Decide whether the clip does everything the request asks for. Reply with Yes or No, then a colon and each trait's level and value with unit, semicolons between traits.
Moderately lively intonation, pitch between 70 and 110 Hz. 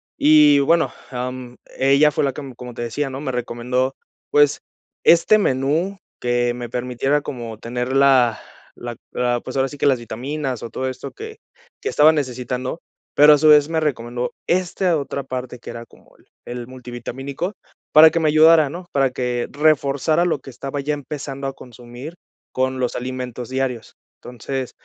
No: average, 3.2 semitones; low, 135 Hz